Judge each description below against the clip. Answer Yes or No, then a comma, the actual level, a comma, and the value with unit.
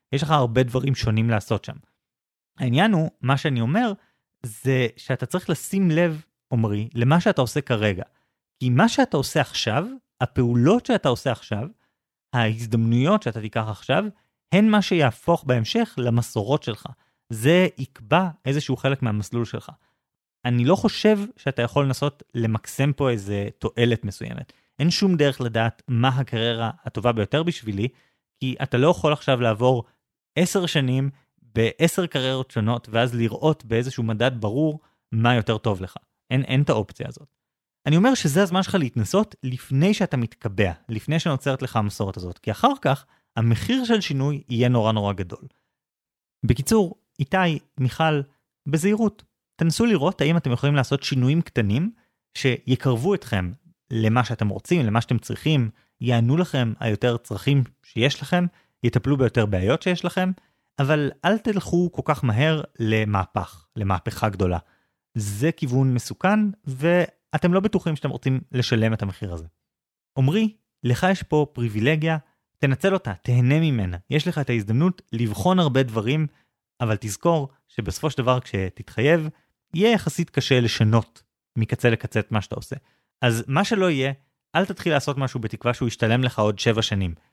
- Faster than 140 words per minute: Yes, fast, 150 wpm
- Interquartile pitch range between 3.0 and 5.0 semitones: No, wide, 5.6 semitones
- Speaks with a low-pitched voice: Yes, low, 130 Hz